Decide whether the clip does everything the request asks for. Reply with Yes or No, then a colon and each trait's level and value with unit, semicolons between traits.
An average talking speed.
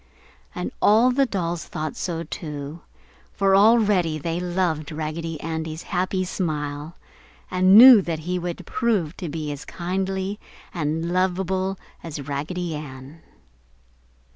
No: slow, 120 wpm